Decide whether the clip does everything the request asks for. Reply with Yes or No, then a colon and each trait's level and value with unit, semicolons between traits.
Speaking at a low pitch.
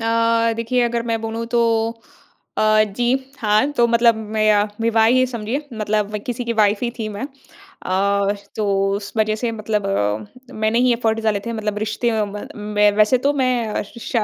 No: high, 225 Hz